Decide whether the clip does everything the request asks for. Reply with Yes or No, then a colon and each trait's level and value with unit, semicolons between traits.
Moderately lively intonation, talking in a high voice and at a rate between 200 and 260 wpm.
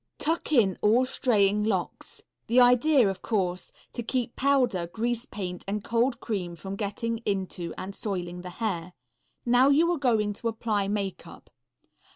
No: average, 4.2 semitones; high, 215 Hz; average, 160 wpm